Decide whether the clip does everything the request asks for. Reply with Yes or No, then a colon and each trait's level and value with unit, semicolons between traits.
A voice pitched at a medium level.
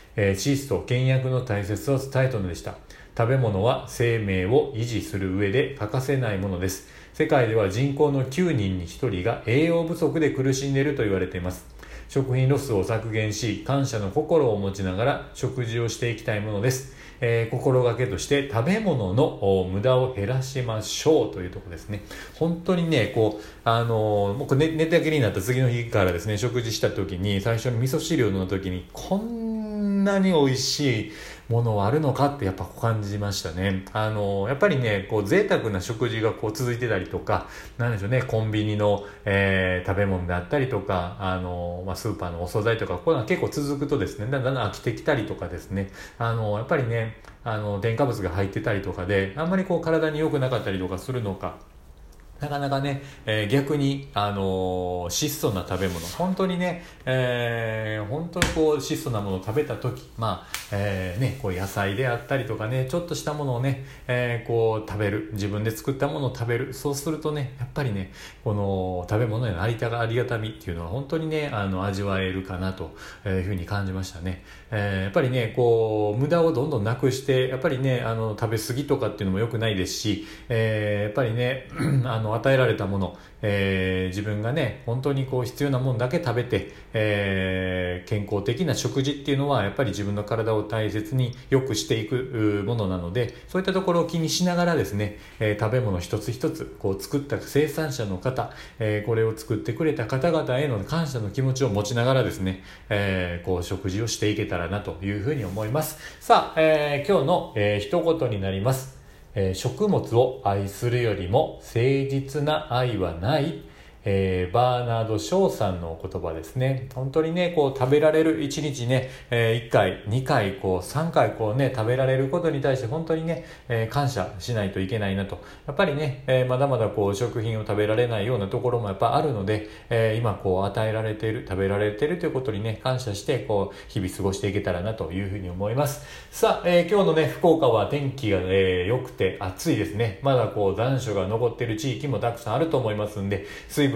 No: low, 115 Hz